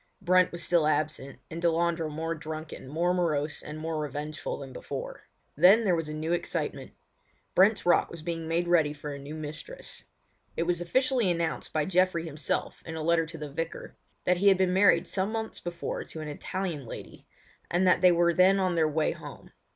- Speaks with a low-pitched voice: No, medium, 170 Hz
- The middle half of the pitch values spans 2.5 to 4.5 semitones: Yes, average, 2.8 semitones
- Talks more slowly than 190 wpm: No, average, 195 wpm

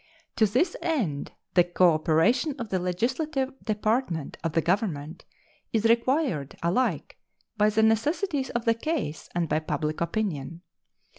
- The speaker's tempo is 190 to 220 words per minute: No, slow, 135 wpm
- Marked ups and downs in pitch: Yes, wide, 7.4 semitones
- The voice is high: Yes, high, 210 Hz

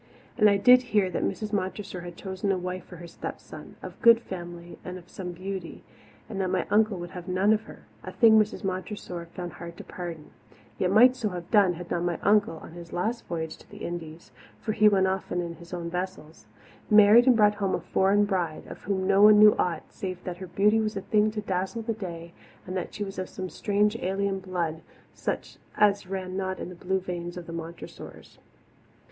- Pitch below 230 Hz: Yes, high, 190 Hz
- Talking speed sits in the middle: No, fast, 220 wpm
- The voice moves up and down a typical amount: Yes, average, 3.0 semitones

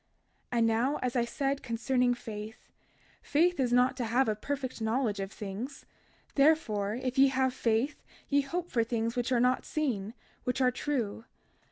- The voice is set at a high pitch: Yes, very high, 250 Hz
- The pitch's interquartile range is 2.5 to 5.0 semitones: Yes, average, 3.1 semitones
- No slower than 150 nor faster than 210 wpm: Yes, average, 170 wpm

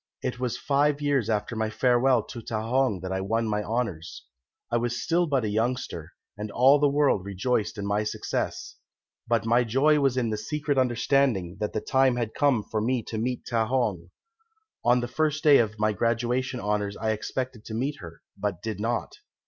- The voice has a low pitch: Yes, low, 115 Hz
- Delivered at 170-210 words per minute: Yes, average, 195 wpm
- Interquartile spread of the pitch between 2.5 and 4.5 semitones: Yes, average, 3.6 semitones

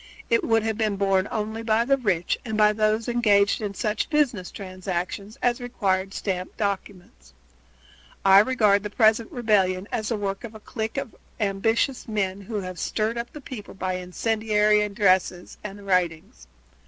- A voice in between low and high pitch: No, high, 210 Hz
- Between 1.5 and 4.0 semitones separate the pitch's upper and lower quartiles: Yes, narrow, 2.6 semitones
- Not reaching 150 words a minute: No, average, 165 wpm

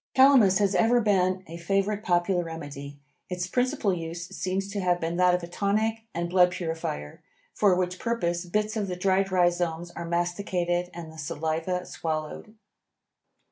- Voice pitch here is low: No, medium, 180 Hz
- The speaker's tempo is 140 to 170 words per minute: Yes, average, 160 wpm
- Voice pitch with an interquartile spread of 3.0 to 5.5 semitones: No, narrow, 2.5 semitones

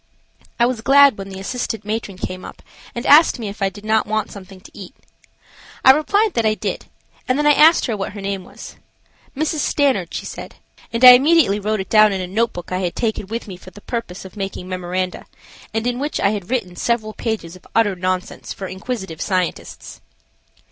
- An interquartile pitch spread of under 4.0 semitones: No, average, 4.3 semitones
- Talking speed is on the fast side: Yes, fast, 210 wpm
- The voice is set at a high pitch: Yes, high, 215 Hz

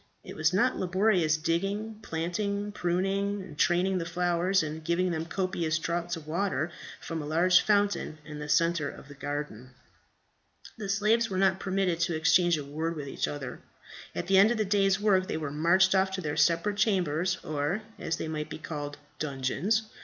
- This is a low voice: No, medium, 175 Hz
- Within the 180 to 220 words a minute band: Yes, average, 185 wpm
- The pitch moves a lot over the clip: No, average, 3.8 semitones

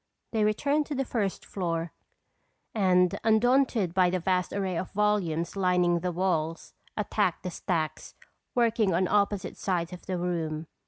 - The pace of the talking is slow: No, average, 150 wpm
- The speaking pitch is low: No, medium, 185 Hz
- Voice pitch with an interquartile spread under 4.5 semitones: Yes, average, 3.3 semitones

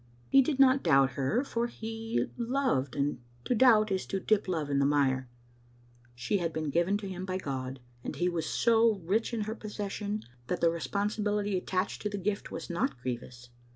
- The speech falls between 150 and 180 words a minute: No, average, 190 wpm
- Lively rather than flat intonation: Yes, wide, 7.1 semitones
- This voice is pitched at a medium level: No, high, 195 Hz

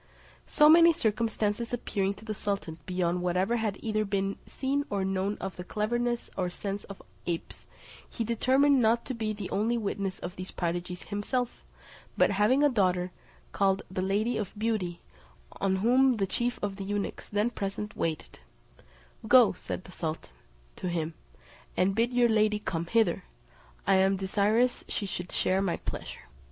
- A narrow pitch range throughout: No, average, 3.5 semitones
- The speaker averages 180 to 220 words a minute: No, average, 165 wpm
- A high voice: Yes, high, 205 Hz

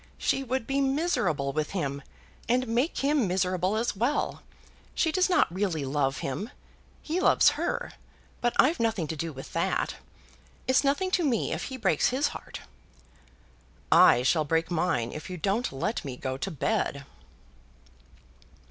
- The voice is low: No, high, 200 Hz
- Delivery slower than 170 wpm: Yes, average, 155 wpm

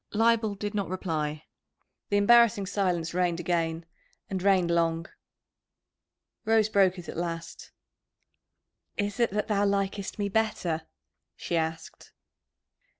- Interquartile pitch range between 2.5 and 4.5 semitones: Yes, average, 3.5 semitones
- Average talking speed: No, slow, 120 wpm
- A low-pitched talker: No, high, 190 Hz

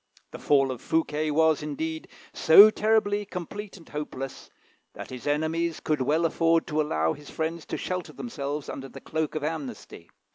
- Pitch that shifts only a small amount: Yes, narrow, 2.3 semitones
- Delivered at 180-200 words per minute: No, average, 170 wpm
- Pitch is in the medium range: Yes, medium, 155 Hz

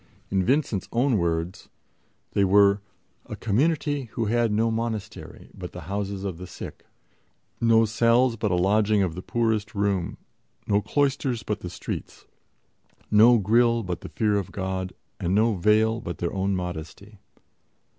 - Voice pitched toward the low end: Yes, low, 105 Hz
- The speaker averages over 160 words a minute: No, average, 155 wpm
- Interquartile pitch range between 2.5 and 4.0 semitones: Yes, average, 3.4 semitones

